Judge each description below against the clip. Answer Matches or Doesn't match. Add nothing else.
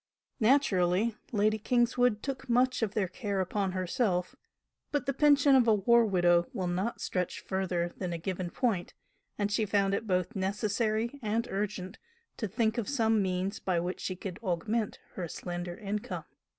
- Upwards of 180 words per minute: Doesn't match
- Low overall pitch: Doesn't match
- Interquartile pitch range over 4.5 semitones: Doesn't match